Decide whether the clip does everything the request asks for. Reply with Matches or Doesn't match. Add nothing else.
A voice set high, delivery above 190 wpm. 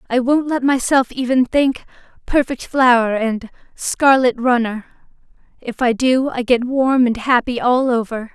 Doesn't match